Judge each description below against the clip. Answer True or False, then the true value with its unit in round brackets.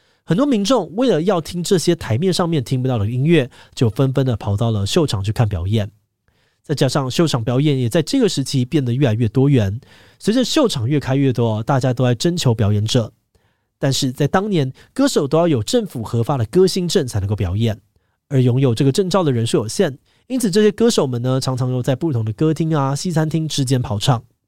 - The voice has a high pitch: False (135 Hz)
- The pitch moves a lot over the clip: True (6.1 semitones)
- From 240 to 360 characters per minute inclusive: True (320 characters per minute)